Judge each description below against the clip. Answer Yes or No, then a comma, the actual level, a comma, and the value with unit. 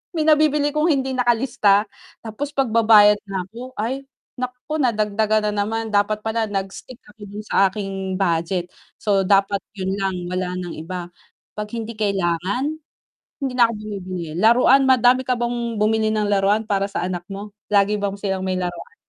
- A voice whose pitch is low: No, high, 210 Hz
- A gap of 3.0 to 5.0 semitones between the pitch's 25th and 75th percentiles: Yes, average, 3.6 semitones